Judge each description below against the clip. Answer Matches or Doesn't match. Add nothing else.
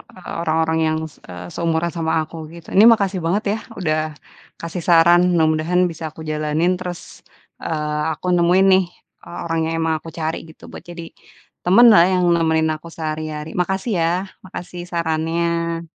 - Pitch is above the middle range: Doesn't match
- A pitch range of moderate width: Doesn't match